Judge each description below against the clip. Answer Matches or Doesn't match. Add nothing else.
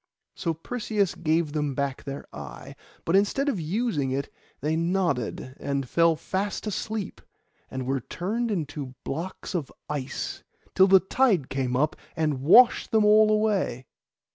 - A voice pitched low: Doesn't match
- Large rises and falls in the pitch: Matches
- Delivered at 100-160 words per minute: Matches